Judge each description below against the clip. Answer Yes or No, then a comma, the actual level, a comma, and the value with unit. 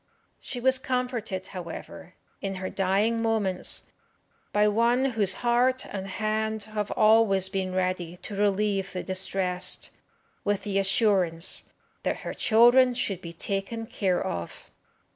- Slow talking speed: Yes, slow, 130 wpm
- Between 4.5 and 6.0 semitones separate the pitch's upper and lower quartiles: No, average, 3.1 semitones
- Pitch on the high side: Yes, high, 205 Hz